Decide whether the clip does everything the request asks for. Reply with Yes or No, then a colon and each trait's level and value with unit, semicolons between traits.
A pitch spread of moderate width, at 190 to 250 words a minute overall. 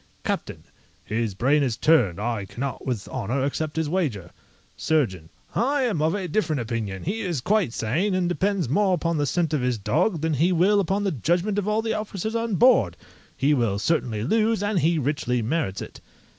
No: wide, 8.3 semitones; average, 195 wpm